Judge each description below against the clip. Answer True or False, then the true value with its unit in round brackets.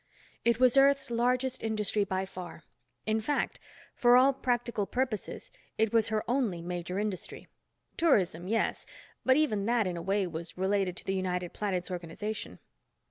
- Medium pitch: False (210 Hz)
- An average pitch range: True (4.8 semitones)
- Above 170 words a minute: False (155 wpm)